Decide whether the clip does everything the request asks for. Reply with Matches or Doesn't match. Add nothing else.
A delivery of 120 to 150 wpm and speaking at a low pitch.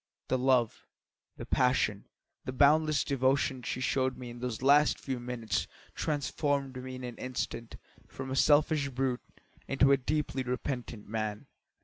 Matches